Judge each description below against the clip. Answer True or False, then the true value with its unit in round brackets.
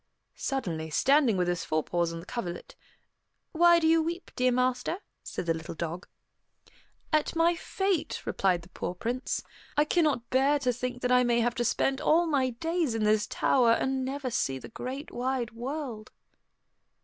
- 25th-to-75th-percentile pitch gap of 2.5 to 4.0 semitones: False (5.4 semitones)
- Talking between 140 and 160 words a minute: False (175 wpm)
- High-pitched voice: True (250 Hz)